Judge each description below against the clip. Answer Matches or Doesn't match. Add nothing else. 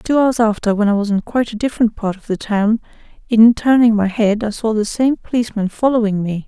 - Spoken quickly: Matches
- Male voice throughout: Doesn't match